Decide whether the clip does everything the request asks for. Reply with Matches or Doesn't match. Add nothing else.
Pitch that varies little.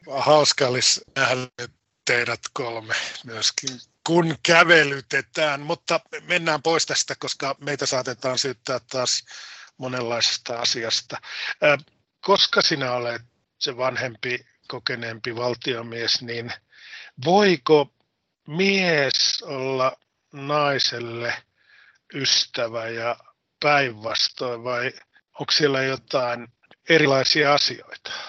Doesn't match